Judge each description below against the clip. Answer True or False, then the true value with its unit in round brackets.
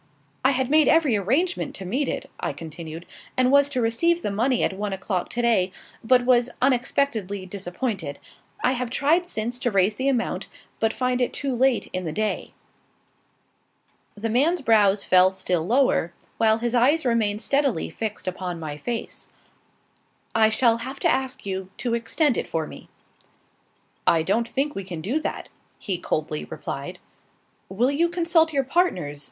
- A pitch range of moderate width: False (5.7 semitones)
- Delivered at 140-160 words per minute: False (170 wpm)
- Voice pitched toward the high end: True (230 Hz)